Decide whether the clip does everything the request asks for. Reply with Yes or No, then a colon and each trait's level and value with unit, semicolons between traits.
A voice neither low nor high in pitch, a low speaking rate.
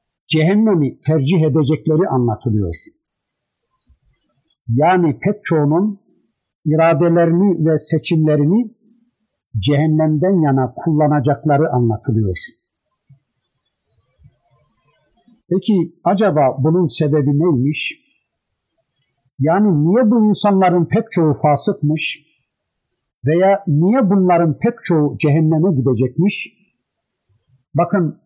Yes: medium, 155 Hz; slow, 70 wpm